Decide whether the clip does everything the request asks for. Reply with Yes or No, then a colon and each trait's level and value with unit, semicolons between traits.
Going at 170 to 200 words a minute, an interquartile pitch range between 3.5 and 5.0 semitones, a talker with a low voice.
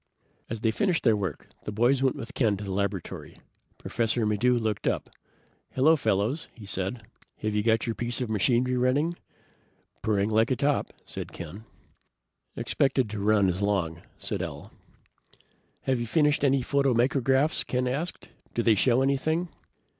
No: average, 160 wpm; average, 4.1 semitones; low, 120 Hz